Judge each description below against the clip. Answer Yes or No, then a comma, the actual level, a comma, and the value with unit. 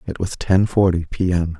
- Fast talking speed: Yes, fast, 225 wpm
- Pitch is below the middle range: Yes, very low, 90 Hz